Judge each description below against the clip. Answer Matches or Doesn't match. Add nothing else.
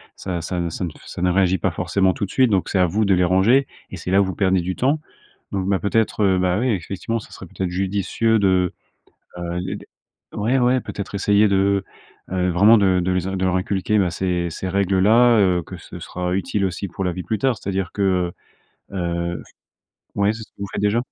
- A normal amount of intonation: Doesn't match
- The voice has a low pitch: Matches